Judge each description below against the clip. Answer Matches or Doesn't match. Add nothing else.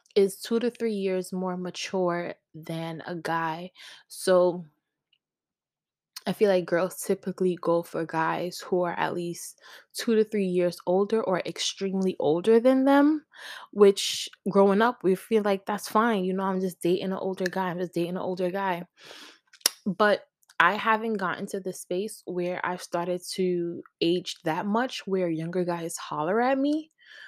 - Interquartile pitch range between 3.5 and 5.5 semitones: Doesn't match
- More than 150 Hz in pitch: Matches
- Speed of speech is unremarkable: Matches